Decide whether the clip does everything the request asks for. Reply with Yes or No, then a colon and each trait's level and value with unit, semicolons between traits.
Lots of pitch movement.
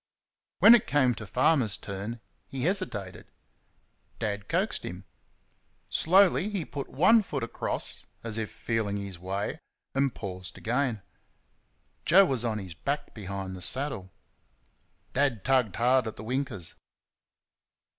Yes: wide, 5.8 semitones